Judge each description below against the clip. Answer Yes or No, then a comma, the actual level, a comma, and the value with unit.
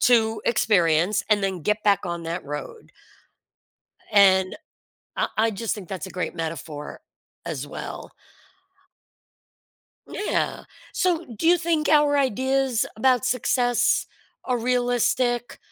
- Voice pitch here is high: Yes, high, 225 Hz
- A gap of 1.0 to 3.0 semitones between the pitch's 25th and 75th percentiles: No, average, 5.3 semitones